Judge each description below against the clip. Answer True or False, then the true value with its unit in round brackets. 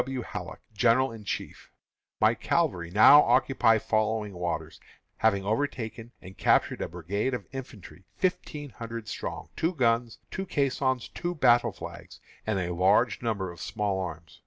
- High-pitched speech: False (115 Hz)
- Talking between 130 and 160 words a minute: True (150 wpm)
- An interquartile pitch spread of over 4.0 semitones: True (4.9 semitones)